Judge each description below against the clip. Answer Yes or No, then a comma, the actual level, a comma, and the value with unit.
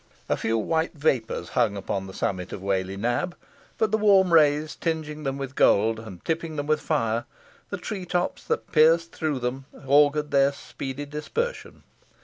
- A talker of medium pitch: Yes, medium, 145 Hz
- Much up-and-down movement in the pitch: Yes, wide, 6.2 semitones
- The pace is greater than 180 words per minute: No, average, 165 wpm